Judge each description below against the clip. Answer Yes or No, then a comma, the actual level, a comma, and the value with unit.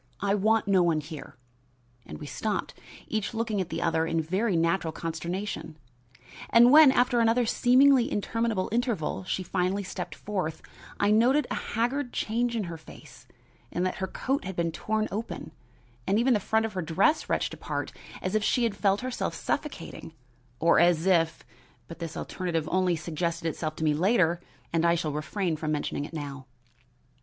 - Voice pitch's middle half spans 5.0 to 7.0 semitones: Yes, average, 5.3 semitones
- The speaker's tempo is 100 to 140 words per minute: No, average, 175 wpm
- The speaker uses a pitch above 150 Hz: Yes, medium, 185 Hz